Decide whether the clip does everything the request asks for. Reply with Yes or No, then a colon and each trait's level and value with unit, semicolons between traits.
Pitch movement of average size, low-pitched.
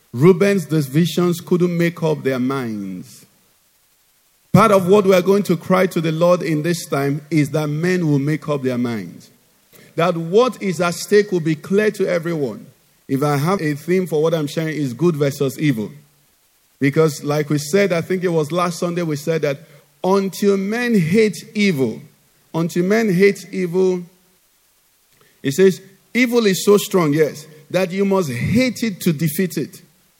No: average, 4.0 semitones; medium, 175 Hz